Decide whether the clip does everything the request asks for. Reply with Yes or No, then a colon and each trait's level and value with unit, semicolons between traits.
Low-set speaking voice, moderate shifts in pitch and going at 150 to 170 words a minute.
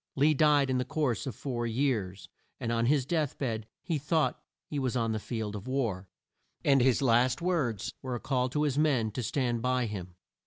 No: low, 125 Hz; average, 3.7 semitones; fast, 205 wpm